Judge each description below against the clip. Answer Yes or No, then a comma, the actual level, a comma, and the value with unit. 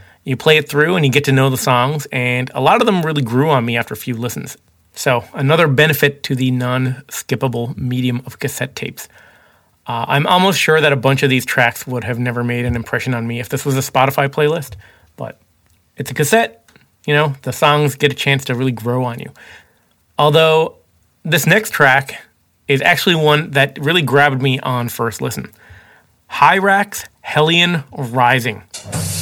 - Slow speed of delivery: No, average, 190 wpm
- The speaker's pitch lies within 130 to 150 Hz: Yes, low, 135 Hz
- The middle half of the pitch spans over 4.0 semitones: No, average, 3.3 semitones